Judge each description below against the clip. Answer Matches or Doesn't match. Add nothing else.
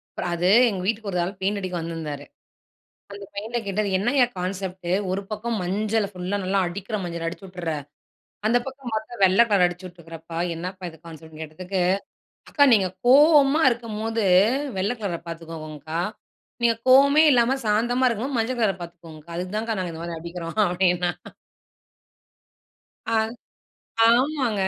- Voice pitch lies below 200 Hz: Matches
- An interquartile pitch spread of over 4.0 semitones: Matches